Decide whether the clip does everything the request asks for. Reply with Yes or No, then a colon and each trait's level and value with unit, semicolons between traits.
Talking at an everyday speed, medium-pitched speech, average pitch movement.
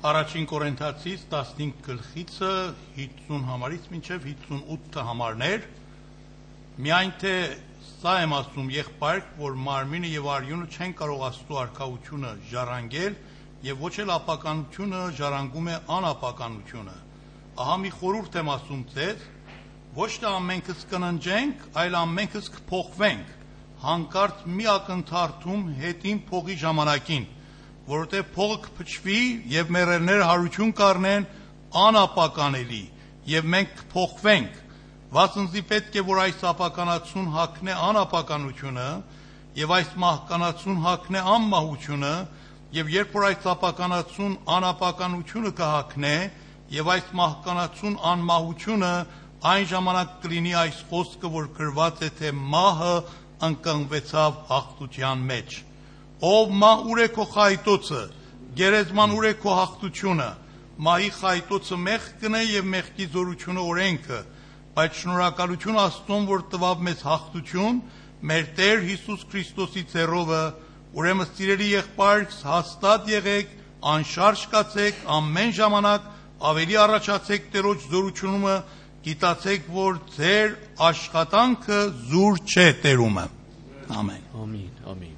No: slow, 105 wpm; medium, 175 Hz; average, 4.4 semitones